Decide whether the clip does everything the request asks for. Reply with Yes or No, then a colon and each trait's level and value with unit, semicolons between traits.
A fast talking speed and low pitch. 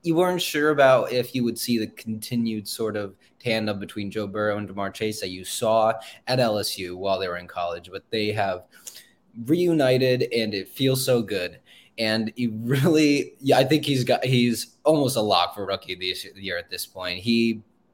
No: average, 195 wpm; low, 115 Hz